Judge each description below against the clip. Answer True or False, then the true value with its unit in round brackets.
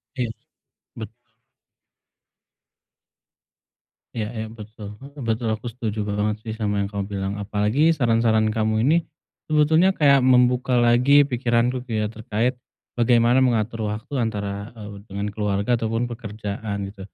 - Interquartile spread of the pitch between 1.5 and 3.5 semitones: True (2.8 semitones)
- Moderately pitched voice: False (115 Hz)